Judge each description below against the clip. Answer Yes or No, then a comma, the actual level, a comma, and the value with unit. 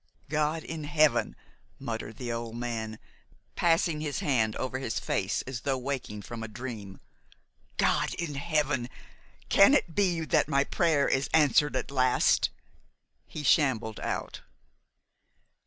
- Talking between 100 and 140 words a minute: Yes, slow, 135 wpm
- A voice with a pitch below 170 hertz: Yes, low, 135 Hz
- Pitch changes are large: No, average, 4.6 semitones